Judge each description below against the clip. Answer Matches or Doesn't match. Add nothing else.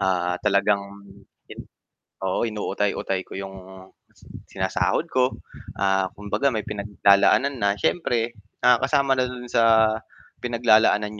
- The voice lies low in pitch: Matches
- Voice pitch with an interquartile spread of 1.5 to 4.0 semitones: Matches